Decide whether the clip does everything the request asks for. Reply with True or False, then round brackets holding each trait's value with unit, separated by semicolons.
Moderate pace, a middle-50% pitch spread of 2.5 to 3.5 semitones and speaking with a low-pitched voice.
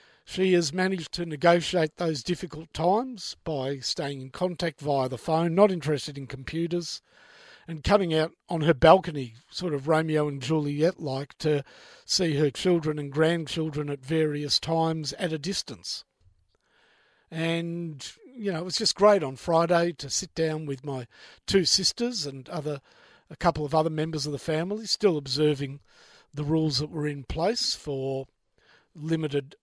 False (160 wpm; 3.1 semitones; 160 Hz)